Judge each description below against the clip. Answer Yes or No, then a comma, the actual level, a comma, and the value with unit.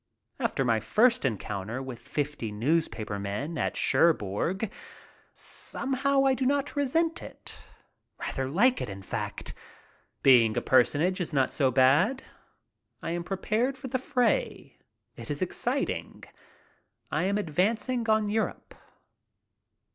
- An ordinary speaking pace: No, slow, 130 wpm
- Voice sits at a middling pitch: Yes, medium, 175 Hz